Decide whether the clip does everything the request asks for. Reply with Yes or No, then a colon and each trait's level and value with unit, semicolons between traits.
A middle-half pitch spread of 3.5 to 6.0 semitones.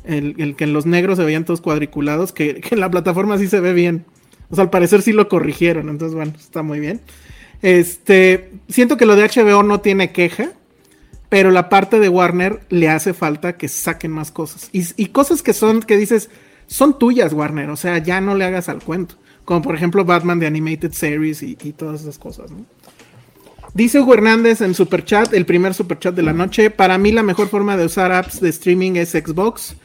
Yes: average, 4.1 semitones